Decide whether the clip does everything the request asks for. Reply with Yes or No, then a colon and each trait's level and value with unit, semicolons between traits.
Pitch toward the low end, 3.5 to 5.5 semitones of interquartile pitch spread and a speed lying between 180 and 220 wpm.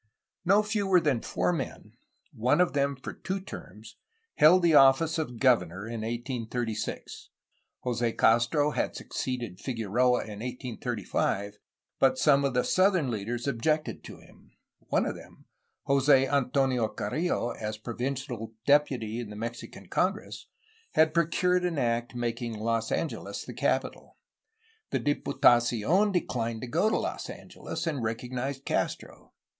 No: low, 125 Hz; average, 4.4 semitones; slow, 135 wpm